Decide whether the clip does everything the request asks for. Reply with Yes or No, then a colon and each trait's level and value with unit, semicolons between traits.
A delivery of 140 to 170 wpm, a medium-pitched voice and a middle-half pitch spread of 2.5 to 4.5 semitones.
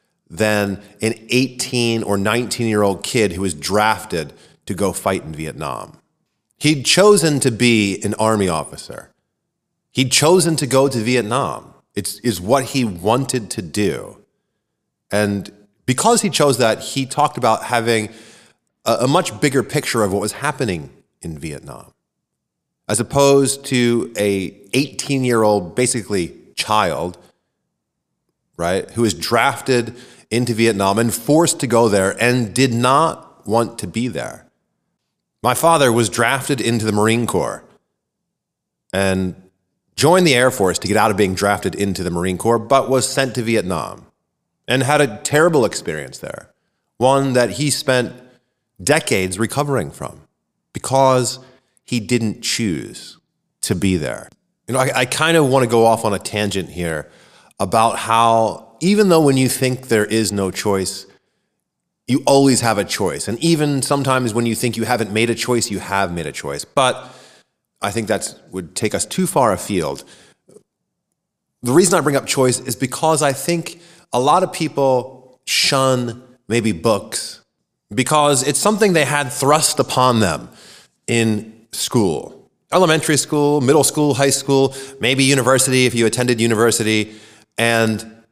No: average, 150 wpm; low, 120 Hz; average, 4.1 semitones